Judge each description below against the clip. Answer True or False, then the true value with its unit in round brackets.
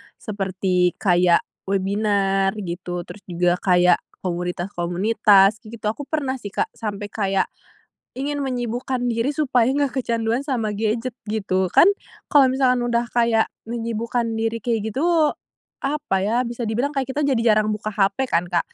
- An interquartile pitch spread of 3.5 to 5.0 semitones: True (4.2 semitones)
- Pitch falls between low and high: False (220 Hz)